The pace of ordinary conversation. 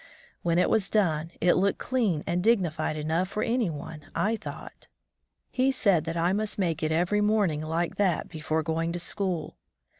Yes: average, 180 wpm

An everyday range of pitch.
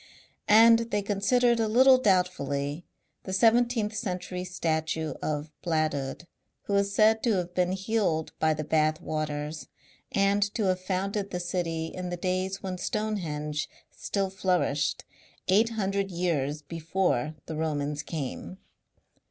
Yes: average, 4.3 semitones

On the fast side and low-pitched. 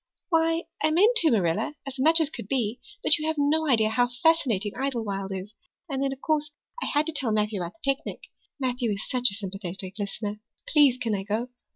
No: fast, 210 wpm; very high, 250 Hz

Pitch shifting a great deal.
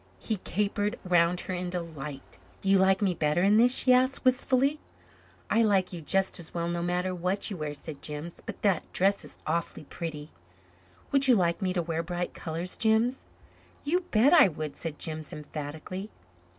No: average, 4.2 semitones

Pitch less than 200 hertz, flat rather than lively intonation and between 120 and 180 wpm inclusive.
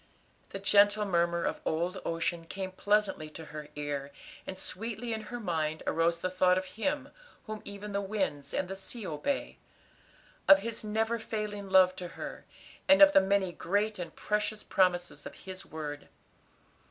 No: high, 190 Hz; average, 3.6 semitones; average, 165 wpm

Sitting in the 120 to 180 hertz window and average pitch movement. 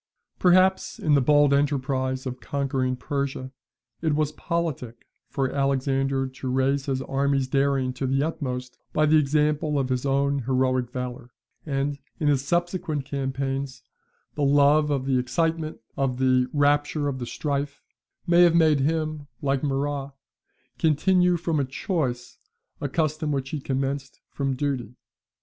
No: medium, 140 Hz; narrow, 2.3 semitones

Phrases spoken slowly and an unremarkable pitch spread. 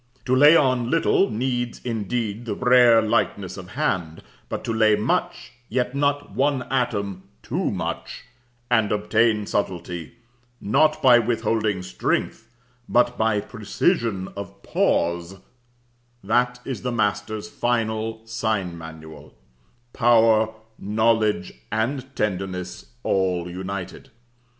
Yes: slow, 110 wpm; average, 3.6 semitones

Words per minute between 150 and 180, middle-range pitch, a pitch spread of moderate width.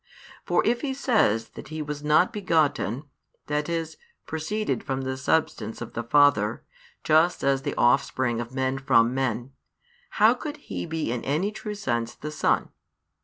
Yes: average, 165 wpm; medium, 145 Hz; average, 5.0 semitones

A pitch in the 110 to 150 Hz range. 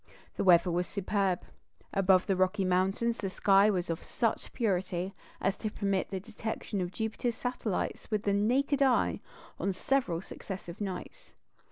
No: high, 195 Hz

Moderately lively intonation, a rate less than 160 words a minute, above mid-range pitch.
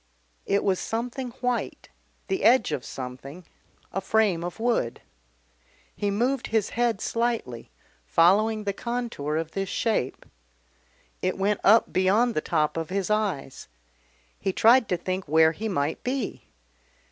No: wide, 5.8 semitones; average, 140 wpm; high, 200 Hz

